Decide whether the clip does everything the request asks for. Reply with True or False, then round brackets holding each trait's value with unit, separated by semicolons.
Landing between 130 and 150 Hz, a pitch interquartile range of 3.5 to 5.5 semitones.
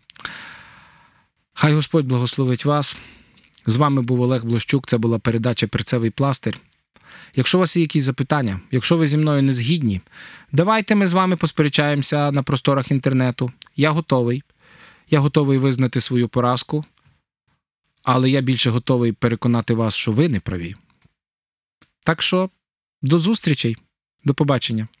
True (135 Hz; 3.9 semitones)